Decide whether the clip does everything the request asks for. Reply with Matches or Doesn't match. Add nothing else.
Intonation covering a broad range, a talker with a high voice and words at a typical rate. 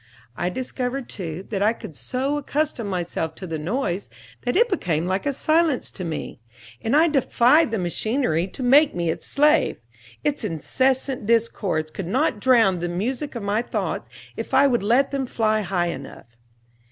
Matches